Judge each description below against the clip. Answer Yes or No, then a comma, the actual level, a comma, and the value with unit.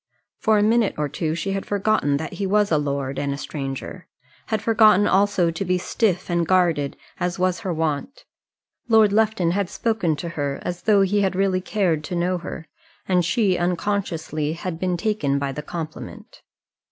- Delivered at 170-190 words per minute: Yes, average, 185 wpm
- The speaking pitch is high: No, medium, 180 Hz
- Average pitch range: Yes, average, 4.2 semitones